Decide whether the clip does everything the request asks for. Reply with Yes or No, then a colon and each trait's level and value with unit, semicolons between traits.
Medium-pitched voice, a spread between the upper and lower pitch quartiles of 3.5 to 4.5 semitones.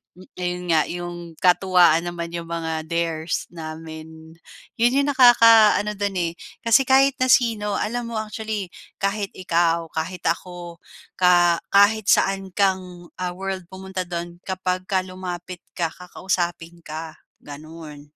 No: medium, 180 Hz; average, 3.0 semitones